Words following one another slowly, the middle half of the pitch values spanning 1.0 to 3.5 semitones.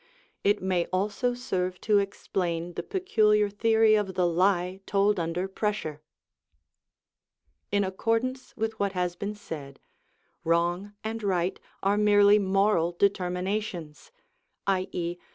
Yes: slow, 115 wpm; average, 2.9 semitones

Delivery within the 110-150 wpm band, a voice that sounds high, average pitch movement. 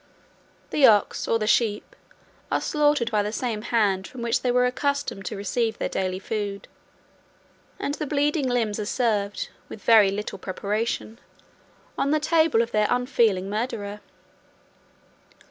Yes: average, 145 wpm; high, 225 Hz; average, 3.4 semitones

